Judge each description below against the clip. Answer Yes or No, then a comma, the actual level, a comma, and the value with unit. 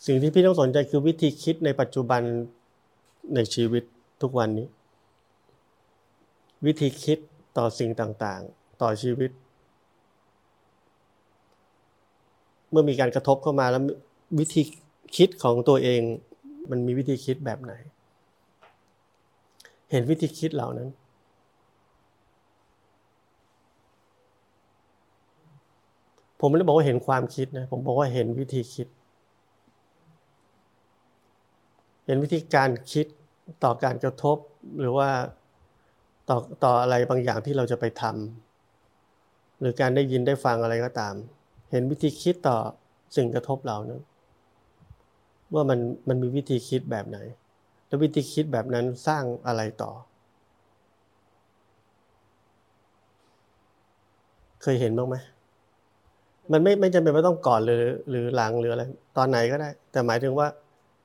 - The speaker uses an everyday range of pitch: Yes, average, 4.0 semitones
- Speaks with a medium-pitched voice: No, low, 125 Hz